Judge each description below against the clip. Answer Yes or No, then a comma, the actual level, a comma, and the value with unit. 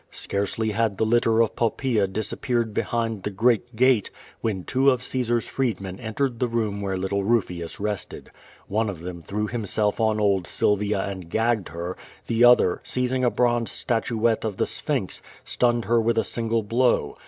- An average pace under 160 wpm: No, average, 170 wpm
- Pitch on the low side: Yes, low, 110 Hz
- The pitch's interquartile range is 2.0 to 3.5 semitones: Yes, average, 3.0 semitones